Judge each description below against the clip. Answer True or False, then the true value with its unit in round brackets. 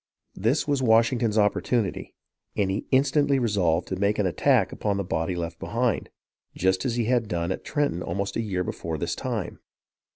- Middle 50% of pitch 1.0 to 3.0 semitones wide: False (4.8 semitones)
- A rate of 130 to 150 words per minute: False (175 wpm)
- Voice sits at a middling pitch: False (105 Hz)